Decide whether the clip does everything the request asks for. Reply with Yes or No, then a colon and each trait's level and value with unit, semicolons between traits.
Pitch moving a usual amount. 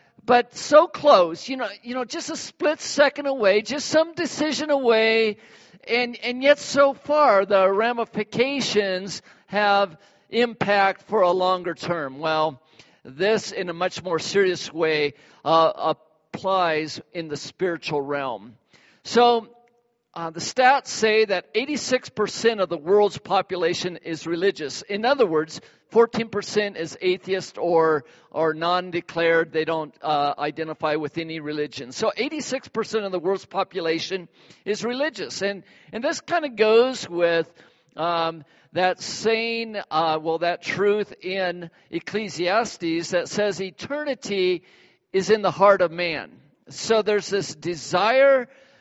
No: wide, 5.8 semitones